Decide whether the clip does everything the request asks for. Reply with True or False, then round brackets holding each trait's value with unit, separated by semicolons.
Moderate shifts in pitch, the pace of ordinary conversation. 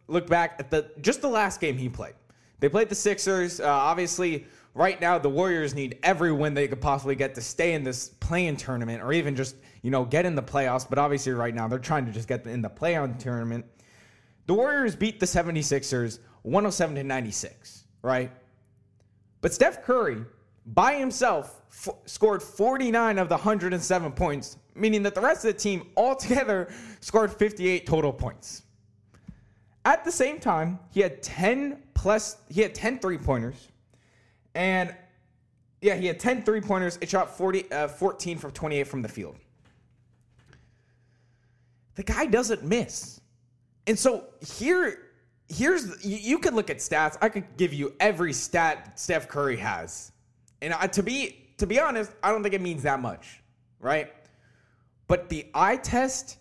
False (8.4 semitones; 170 wpm)